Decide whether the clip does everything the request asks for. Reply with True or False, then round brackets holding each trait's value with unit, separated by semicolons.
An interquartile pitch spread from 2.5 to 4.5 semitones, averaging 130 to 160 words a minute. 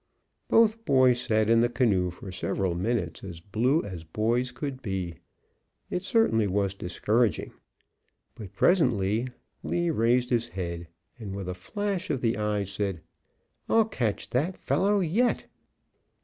False (5.4 semitones; 140 wpm)